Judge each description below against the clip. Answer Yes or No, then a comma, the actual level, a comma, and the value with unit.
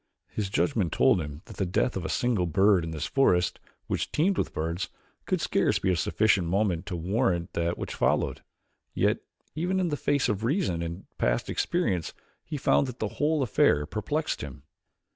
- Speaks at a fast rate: No, average, 185 wpm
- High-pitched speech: No, very low, 95 Hz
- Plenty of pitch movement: Yes, wide, 7.9 semitones